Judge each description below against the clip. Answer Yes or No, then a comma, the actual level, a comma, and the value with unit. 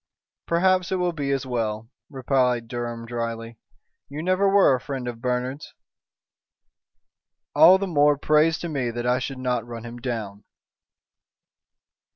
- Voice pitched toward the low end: Yes, low, 130 Hz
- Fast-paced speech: No, average, 145 wpm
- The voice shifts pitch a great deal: No, average, 4.5 semitones